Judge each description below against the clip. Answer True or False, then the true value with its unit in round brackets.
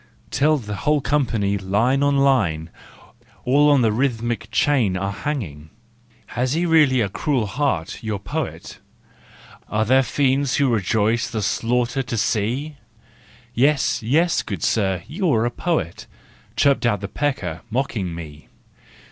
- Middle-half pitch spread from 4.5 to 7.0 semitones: True (5.5 semitones)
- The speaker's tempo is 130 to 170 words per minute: True (145 wpm)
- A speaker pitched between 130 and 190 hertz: False (120 Hz)